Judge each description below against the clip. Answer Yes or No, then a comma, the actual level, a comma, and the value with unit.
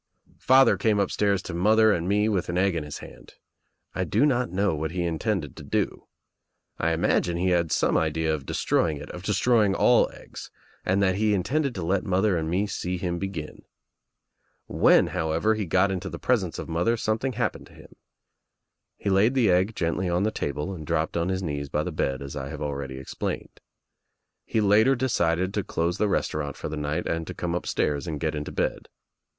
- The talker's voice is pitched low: Yes, very low, 90 Hz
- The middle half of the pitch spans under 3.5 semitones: No, average, 4.3 semitones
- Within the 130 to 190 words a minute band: No, average, 200 wpm